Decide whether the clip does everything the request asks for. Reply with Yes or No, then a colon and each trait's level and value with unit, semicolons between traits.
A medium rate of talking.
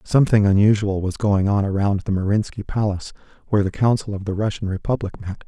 Yes: average, 185 wpm